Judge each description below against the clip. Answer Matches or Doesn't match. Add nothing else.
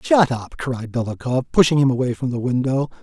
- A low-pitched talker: Matches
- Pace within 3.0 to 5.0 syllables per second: Doesn't match